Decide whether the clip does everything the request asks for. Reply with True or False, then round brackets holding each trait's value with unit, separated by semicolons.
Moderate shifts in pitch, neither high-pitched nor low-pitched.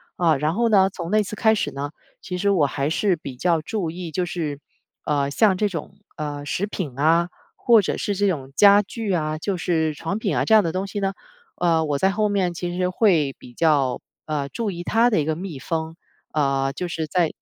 True (4.5 semitones; 170 Hz)